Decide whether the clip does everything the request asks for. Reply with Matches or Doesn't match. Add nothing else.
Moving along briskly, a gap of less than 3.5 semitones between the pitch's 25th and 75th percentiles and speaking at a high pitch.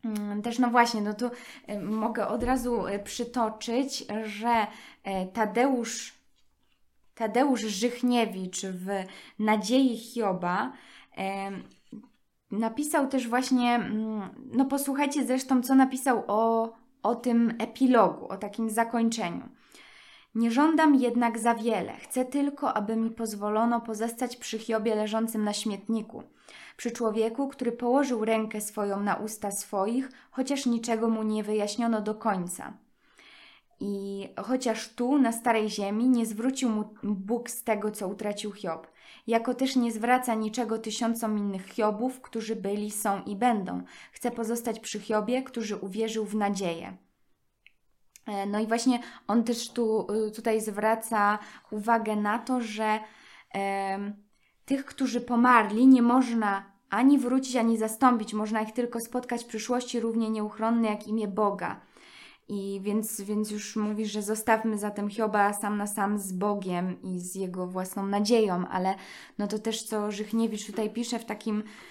Doesn't match